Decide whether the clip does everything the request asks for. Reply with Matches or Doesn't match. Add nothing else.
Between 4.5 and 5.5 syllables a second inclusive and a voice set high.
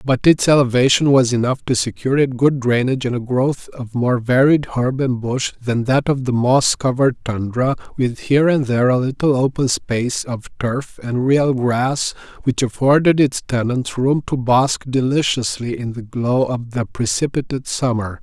Doesn't match